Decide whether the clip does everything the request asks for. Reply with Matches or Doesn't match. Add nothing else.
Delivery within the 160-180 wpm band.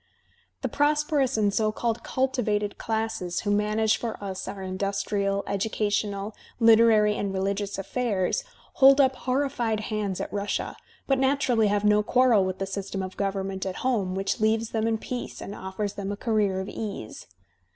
Matches